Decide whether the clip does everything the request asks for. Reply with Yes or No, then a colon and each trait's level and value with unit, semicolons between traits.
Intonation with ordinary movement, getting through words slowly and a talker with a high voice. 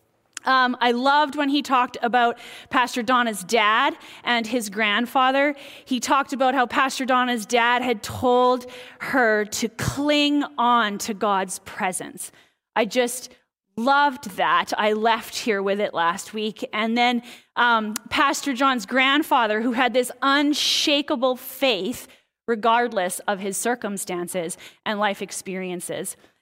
Yes: average, 3.6 semitones; slow, 130 wpm; high, 245 Hz